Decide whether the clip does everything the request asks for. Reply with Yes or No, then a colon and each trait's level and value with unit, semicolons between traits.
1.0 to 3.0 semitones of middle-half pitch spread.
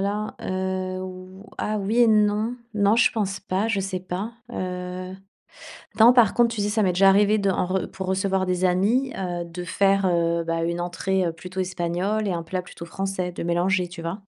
Yes: narrow, 2.5 semitones